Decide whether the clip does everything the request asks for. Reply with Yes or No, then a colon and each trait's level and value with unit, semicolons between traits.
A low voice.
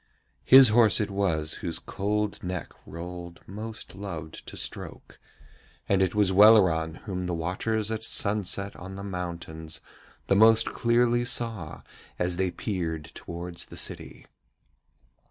Yes: very low, 95 Hz